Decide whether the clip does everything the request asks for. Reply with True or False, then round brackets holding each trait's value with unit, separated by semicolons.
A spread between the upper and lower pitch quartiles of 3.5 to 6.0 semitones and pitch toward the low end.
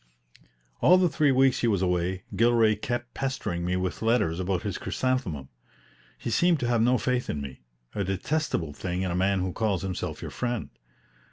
True (5.4 semitones; 105 Hz)